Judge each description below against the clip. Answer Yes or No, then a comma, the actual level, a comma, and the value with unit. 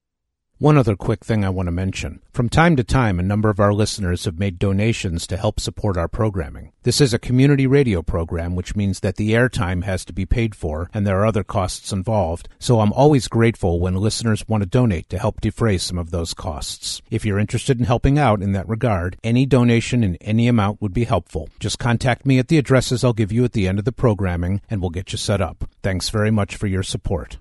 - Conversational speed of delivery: No, fast, 235 wpm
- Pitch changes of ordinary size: Yes, average, 4.0 semitones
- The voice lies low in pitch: Yes, low, 105 Hz